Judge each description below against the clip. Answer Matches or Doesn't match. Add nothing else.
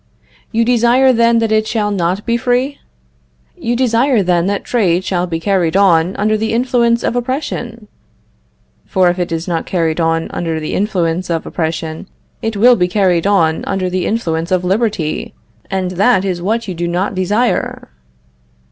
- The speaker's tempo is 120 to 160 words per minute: Doesn't match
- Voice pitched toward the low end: Doesn't match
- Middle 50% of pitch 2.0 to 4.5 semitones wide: Doesn't match